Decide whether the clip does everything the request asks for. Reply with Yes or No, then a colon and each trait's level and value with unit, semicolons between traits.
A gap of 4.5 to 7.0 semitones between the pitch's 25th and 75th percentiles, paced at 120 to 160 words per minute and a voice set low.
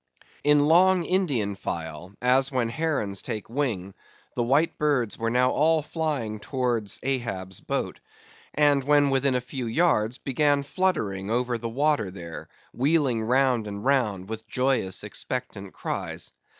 Yes: average, 5.1 semitones; average, 140 wpm; low, 125 Hz